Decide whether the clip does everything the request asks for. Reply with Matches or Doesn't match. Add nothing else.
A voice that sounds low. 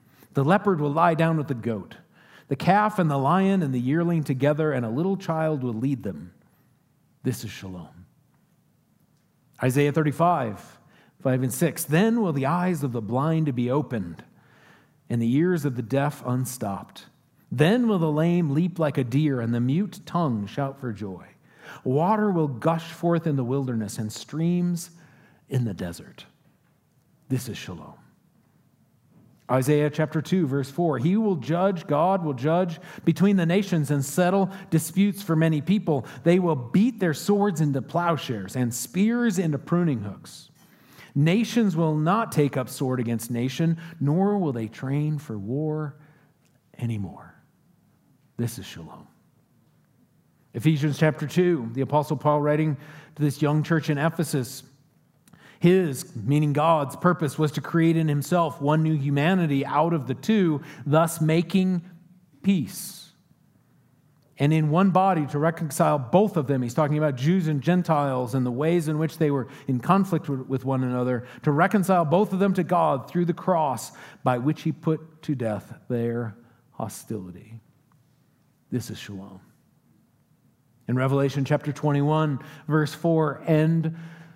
Doesn't match